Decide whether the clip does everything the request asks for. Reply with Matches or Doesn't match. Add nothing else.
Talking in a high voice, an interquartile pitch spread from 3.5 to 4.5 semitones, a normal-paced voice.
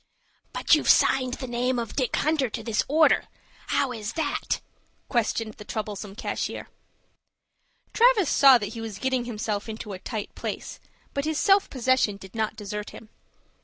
Matches